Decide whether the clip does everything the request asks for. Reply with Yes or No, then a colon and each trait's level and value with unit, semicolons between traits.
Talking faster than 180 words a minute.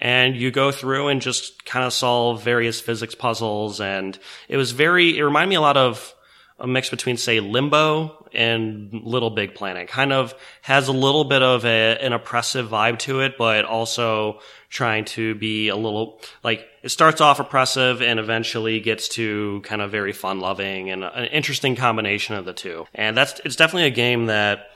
Yes: average, 190 wpm